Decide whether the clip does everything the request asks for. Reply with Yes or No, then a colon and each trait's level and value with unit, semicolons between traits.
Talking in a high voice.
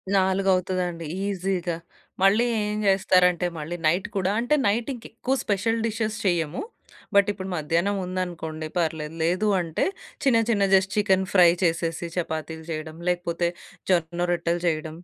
No: medium, 180 Hz